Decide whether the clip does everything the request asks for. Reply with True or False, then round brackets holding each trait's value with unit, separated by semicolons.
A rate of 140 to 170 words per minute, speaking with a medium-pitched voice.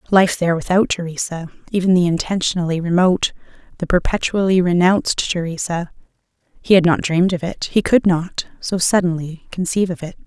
True (145 wpm; 175 Hz)